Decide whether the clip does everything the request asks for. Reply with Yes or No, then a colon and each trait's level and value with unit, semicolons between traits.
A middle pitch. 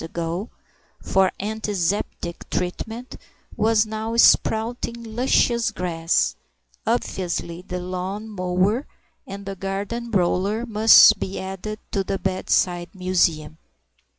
No: high, 195 Hz